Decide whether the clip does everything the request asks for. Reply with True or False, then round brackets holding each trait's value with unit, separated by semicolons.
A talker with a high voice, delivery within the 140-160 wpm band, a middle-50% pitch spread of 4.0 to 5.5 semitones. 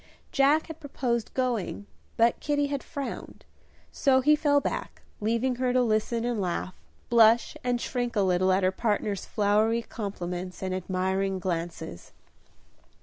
True (225 Hz; 145 wpm; 5.1 semitones)